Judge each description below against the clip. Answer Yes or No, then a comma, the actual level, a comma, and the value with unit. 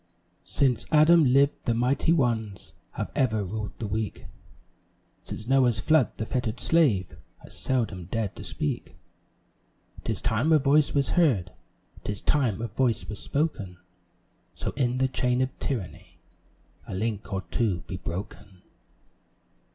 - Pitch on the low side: Yes, low, 115 Hz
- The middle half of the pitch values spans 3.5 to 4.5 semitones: No, average, 4.9 semitones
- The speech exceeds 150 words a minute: No, average, 140 wpm